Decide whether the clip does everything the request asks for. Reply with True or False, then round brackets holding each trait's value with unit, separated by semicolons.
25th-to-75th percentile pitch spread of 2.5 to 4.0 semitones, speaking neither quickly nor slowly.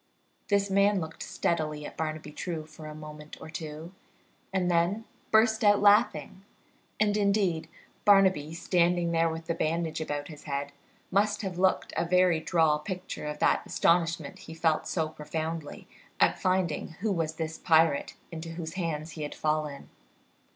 True (3.2 semitones; 160 wpm)